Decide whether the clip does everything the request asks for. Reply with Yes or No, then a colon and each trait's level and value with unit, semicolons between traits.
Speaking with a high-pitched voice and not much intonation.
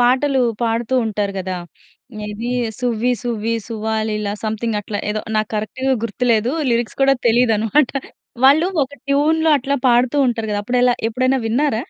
No: high, 235 Hz; average, 3.1 semitones